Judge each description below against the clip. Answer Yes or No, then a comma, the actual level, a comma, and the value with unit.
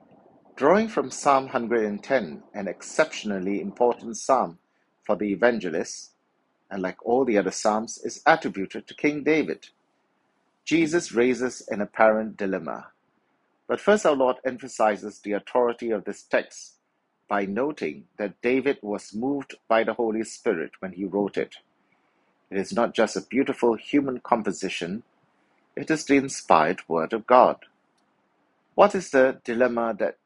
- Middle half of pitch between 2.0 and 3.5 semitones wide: No, average, 4.5 semitones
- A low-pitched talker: Yes, low, 120 Hz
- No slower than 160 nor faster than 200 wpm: No, average, 140 wpm